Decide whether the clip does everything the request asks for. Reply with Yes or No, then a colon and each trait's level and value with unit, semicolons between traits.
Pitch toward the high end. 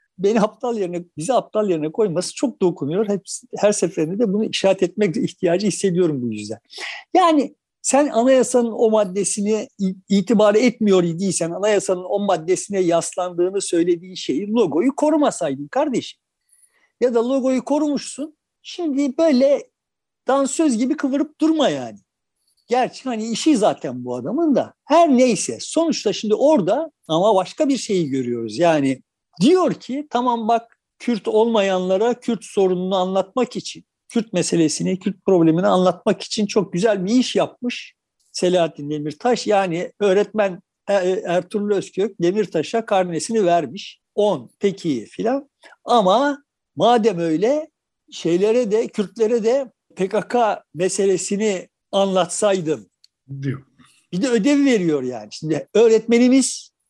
Yes: high, 210 Hz